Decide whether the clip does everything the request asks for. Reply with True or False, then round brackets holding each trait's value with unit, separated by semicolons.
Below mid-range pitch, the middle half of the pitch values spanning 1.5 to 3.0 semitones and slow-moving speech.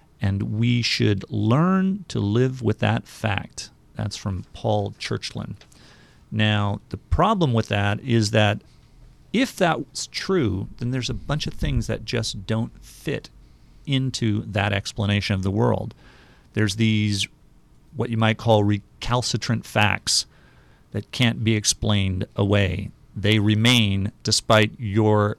True (110 Hz; 2.5 semitones; 130 wpm)